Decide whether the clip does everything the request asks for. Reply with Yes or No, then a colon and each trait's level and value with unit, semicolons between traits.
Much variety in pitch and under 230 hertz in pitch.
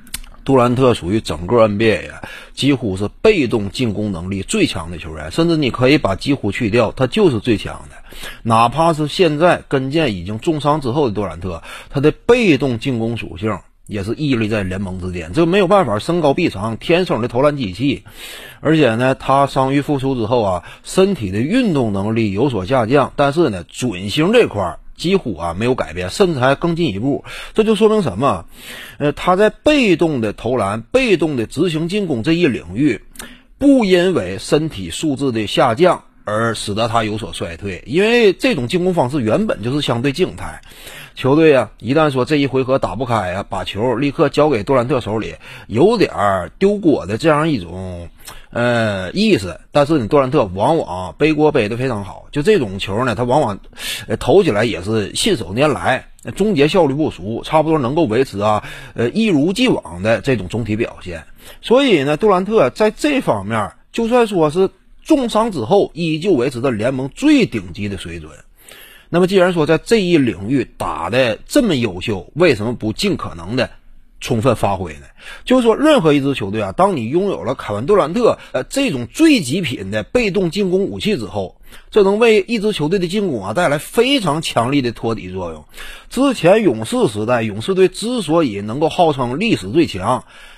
Yes: wide, 8.3 semitones; low, 135 Hz